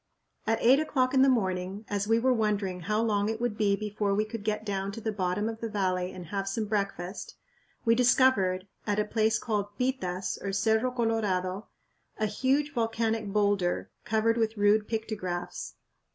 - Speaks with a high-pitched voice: Yes, high, 215 Hz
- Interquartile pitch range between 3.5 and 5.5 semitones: No, narrow, 2.4 semitones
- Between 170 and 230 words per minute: Yes, average, 180 wpm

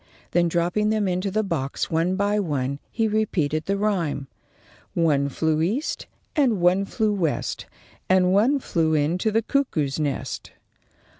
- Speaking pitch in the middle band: Yes, medium, 180 Hz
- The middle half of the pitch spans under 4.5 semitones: No, average, 5.0 semitones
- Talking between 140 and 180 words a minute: Yes, average, 145 wpm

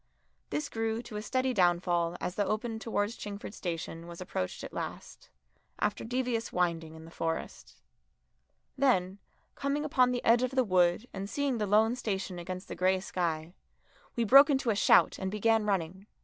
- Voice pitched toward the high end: Yes, high, 205 Hz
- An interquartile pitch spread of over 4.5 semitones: Yes, average, 5.0 semitones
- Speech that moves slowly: No, average, 175 wpm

